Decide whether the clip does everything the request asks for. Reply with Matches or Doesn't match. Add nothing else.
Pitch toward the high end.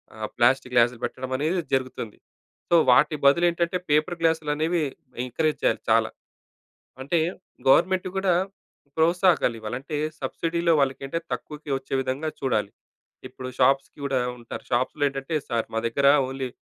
Doesn't match